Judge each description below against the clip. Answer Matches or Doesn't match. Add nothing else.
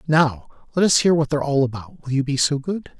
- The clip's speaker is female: Doesn't match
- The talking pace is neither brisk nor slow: Doesn't match